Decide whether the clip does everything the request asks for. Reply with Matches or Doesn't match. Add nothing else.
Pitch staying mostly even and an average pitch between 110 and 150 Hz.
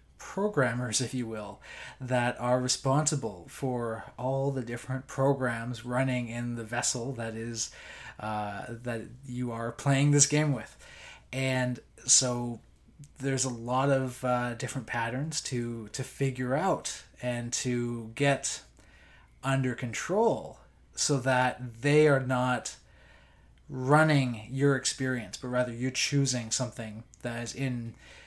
Matches